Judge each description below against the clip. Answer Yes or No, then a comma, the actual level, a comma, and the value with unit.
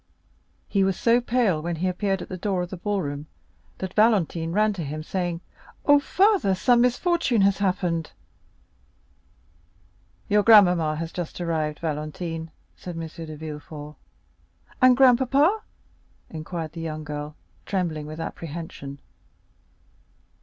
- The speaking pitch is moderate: Yes, medium, 175 Hz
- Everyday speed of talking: No, slow, 130 wpm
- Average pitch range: Yes, average, 4.9 semitones